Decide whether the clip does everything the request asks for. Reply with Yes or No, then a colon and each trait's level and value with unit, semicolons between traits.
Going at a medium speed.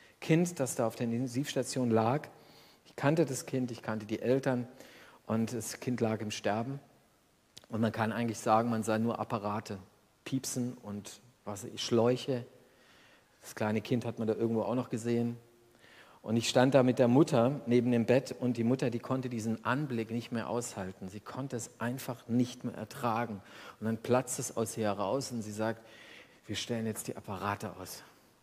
Yes: average, 180 wpm